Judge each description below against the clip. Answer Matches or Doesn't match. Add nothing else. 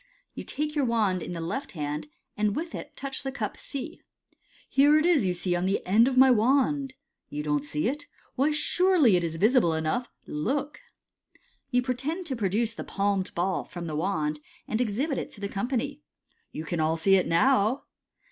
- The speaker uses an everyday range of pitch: Doesn't match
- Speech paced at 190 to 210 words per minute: Matches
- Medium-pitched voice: Doesn't match